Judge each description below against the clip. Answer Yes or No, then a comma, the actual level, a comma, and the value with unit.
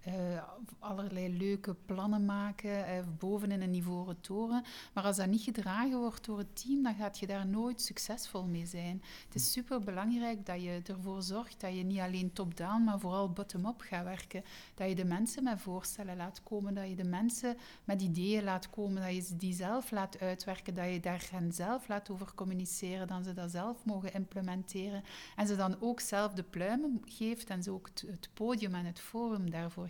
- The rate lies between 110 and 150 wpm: No, fast, 200 wpm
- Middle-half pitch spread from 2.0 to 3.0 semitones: Yes, narrow, 2.6 semitones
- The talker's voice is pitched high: Yes, high, 195 Hz